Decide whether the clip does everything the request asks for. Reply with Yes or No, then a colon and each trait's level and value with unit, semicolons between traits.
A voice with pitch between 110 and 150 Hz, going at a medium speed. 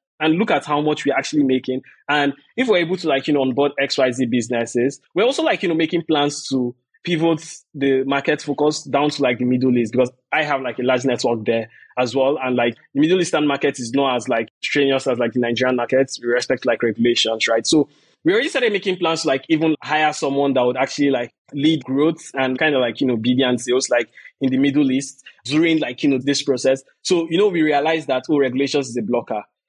No: medium, 140 Hz; fast, 235 wpm